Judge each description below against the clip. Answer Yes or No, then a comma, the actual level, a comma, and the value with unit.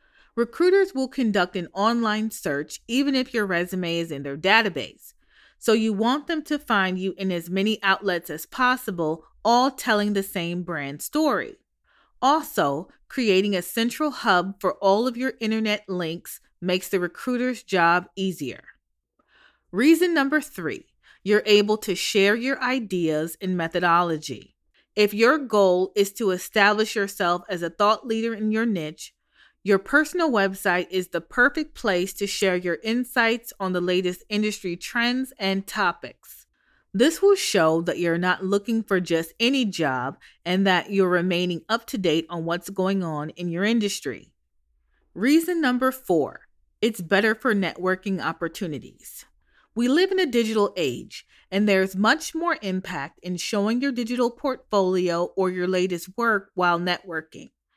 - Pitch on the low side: No, high, 195 Hz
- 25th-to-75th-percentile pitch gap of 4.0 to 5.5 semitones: Yes, average, 4.8 semitones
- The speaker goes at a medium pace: Yes, average, 155 wpm